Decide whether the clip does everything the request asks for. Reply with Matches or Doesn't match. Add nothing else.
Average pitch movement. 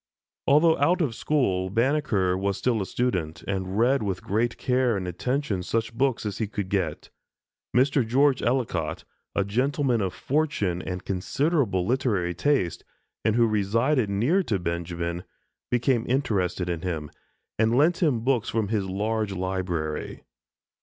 Doesn't match